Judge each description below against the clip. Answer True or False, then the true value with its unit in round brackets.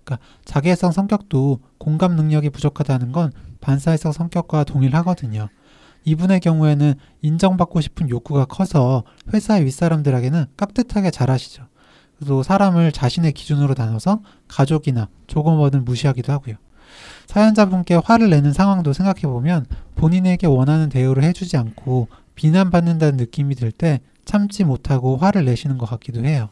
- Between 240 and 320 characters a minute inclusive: False (360 characters per minute)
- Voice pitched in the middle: True (150 Hz)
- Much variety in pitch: False (4.8 semitones)